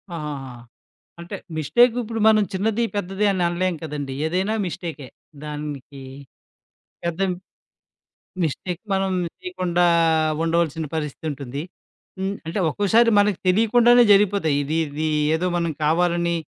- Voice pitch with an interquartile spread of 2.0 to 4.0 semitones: No, average, 4.9 semitones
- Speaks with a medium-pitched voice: Yes, medium, 175 Hz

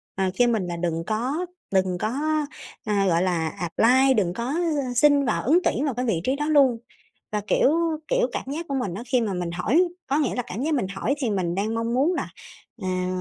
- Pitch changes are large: Yes, wide, 6.9 semitones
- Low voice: No, high, 235 Hz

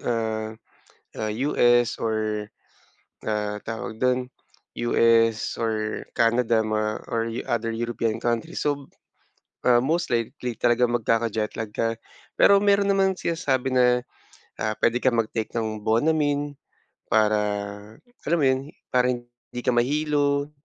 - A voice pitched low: Yes, low, 120 Hz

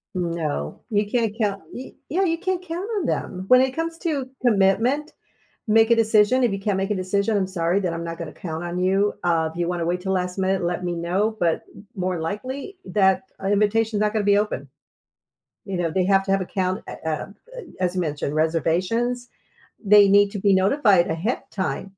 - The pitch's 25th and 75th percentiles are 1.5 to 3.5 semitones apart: No, average, 4.0 semitones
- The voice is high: Yes, high, 195 Hz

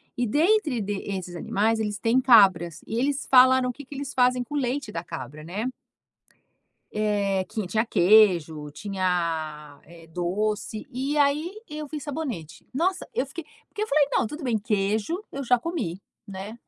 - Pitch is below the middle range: No, high, 220 Hz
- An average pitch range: No, wide, 6.7 semitones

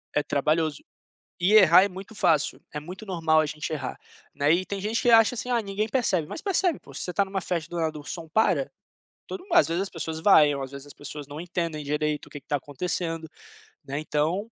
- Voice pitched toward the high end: No, medium, 165 Hz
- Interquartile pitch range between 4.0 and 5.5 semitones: Yes, average, 4.8 semitones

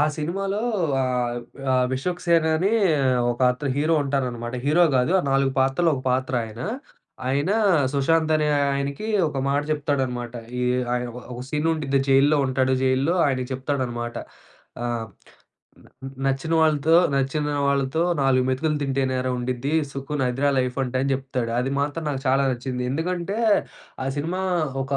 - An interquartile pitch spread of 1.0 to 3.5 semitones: Yes, average, 2.9 semitones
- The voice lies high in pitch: No, low, 135 Hz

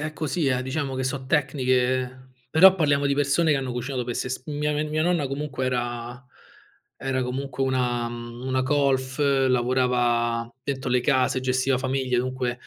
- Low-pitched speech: Yes, low, 130 Hz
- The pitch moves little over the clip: Yes, narrow, 1.9 semitones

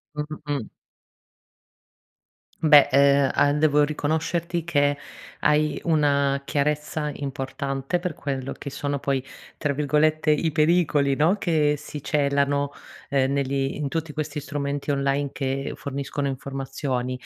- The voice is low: No, medium, 145 Hz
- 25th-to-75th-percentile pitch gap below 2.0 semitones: Yes, narrow, 1.5 semitones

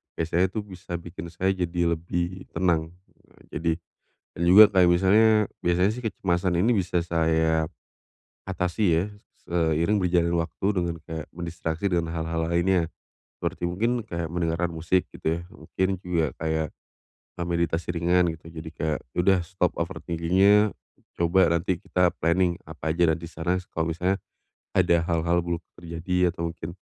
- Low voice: Yes, very low, 85 Hz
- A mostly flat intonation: Yes, narrow, 1.9 semitones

